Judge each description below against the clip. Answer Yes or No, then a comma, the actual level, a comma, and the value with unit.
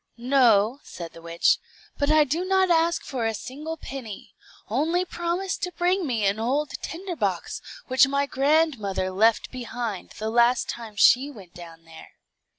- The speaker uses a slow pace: No, average, 160 wpm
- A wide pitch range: Yes, wide, 6.9 semitones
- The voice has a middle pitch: No, very high, 255 Hz